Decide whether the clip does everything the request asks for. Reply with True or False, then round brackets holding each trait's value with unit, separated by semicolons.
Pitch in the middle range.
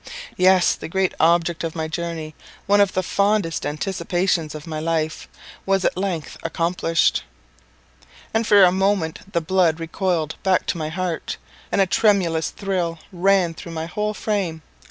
True (175 Hz)